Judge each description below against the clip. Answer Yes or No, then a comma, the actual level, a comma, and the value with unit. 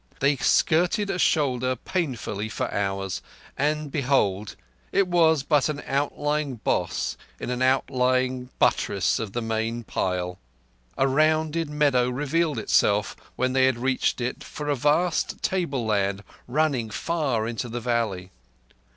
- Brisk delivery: No, slow, 135 wpm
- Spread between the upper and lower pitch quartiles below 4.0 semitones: No, average, 4.7 semitones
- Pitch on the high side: No, low, 130 Hz